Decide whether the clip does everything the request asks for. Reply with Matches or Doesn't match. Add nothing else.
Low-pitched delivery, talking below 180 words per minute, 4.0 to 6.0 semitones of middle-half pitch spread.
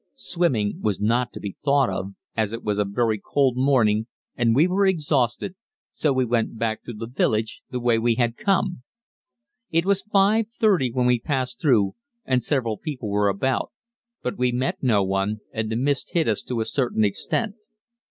Doesn't match